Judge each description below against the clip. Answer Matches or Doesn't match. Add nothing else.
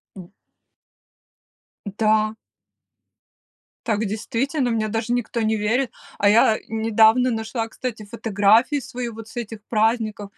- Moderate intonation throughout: Doesn't match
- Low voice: Doesn't match